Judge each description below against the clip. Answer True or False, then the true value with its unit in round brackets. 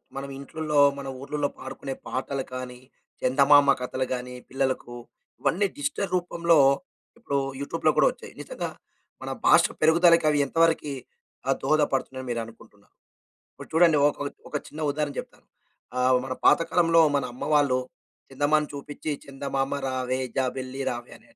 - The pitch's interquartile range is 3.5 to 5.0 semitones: False (3.0 semitones)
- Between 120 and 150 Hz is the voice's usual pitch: True (140 Hz)